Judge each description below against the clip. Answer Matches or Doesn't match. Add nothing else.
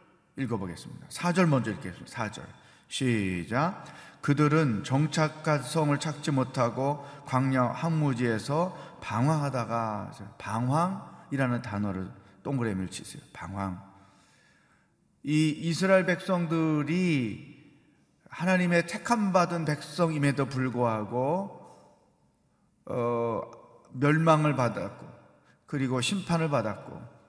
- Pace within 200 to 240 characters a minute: Matches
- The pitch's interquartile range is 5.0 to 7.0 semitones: Matches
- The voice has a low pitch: Doesn't match